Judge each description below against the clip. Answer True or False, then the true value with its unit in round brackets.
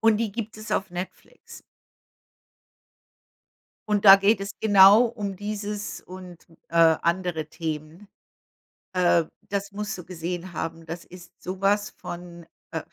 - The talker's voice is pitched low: False (190 Hz)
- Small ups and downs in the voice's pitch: False (3.1 semitones)